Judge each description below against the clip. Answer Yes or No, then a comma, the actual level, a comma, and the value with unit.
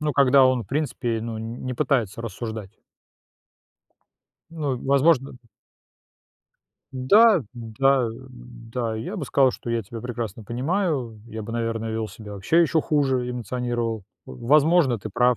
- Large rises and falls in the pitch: No, average, 3.4 semitones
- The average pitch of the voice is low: Yes, low, 120 Hz